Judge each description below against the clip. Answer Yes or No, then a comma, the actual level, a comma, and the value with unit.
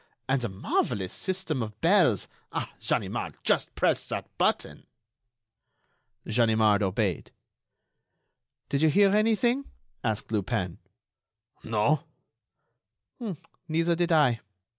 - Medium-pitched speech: No, low, 125 Hz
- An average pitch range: No, wide, 8.1 semitones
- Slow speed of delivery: Yes, slow, 95 wpm